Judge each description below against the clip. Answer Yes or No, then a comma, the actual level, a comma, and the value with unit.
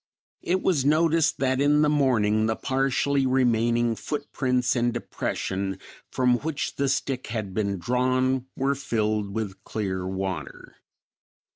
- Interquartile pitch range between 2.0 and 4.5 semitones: Yes, average, 4.1 semitones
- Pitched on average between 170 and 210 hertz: No, low, 125 Hz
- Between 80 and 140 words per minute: Yes, slow, 135 wpm